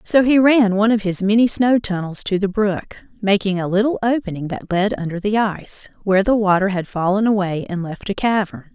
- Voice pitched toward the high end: Yes, high, 200 Hz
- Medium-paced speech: No, fast, 215 wpm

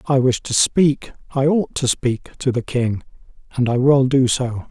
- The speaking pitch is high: No, low, 130 Hz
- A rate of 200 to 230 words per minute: Yes, fast, 205 wpm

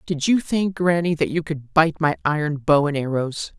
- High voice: No, medium, 155 Hz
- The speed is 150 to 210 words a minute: No, fast, 220 wpm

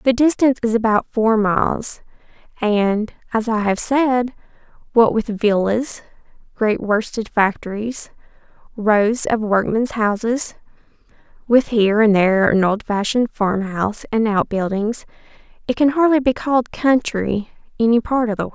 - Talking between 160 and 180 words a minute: No, slow, 135 wpm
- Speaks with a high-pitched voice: Yes, high, 225 Hz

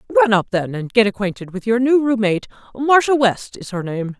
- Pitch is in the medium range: No, high, 220 Hz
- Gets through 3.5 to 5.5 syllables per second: Yes, 5.4 syllables/s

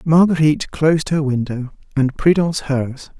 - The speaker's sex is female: No, male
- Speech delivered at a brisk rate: No, slow, 130 wpm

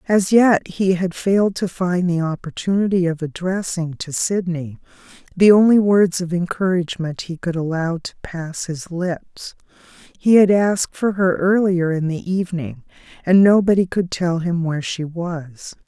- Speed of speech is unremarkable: Yes, average, 160 wpm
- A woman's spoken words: Yes, female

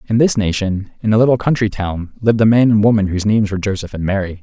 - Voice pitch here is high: No, low, 105 Hz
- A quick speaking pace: Yes, fast, 270 wpm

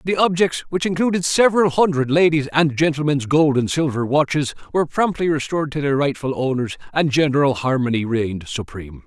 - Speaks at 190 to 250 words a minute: No, average, 165 wpm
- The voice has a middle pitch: Yes, medium, 145 Hz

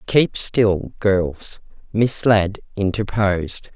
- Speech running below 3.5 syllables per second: Yes, 2.9 syllables/s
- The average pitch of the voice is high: No, low, 100 Hz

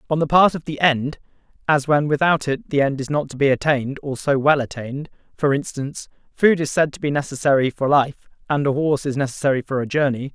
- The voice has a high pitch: No, medium, 140 Hz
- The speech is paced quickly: Yes, fast, 225 wpm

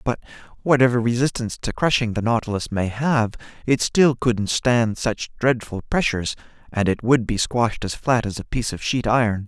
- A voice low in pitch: Yes, low, 115 Hz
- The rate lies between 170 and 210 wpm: Yes, average, 185 wpm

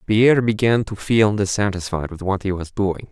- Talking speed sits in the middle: Yes, average, 195 wpm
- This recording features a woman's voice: No, male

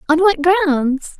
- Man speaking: No, female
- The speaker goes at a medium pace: Yes, average, 150 wpm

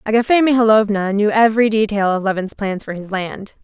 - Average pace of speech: Yes, average, 180 wpm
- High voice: Yes, high, 210 Hz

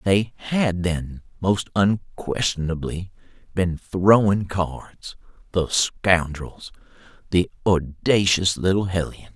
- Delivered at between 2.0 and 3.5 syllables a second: Yes, 3.3 syllables/s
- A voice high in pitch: No, very low, 95 Hz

